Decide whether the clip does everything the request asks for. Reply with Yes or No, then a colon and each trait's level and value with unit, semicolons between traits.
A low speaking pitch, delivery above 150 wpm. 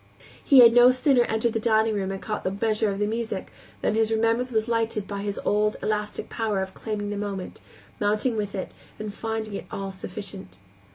No: high, 215 Hz; fast, 205 wpm